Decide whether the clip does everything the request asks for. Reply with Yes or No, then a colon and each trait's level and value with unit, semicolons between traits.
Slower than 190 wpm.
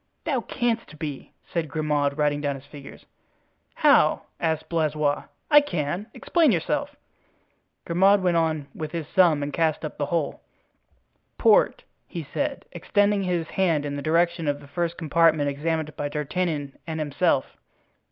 Yes: average, 150 wpm